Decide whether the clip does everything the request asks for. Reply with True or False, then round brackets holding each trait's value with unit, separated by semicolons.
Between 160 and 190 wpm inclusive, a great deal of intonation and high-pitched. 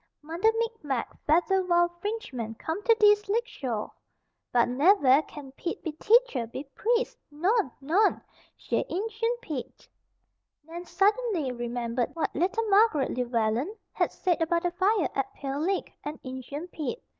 False (145 wpm; 7.5 semitones; 335 Hz)